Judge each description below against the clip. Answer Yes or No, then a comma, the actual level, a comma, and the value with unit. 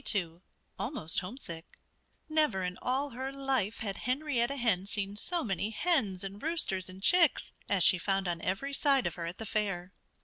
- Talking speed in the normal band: Yes, average, 175 wpm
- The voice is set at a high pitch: Yes, high, 210 Hz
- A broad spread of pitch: Yes, wide, 6.4 semitones